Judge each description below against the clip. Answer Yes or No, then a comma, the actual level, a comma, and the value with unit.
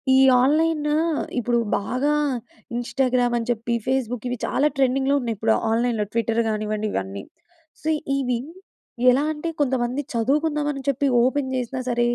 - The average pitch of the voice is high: Yes, very high, 250 Hz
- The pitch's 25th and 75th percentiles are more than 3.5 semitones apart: No, average, 2.9 semitones